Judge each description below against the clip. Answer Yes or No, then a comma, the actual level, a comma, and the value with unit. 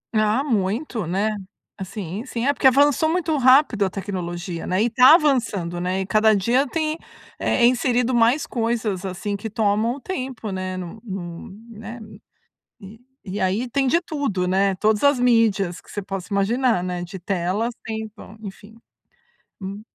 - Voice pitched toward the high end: Yes, high, 215 Hz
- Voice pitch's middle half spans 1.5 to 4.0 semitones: No, average, 4.6 semitones